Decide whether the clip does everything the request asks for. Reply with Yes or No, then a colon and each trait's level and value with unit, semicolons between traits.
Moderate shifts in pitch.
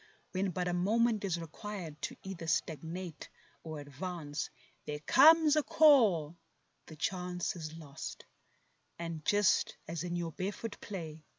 Yes: average, 3.9 semitones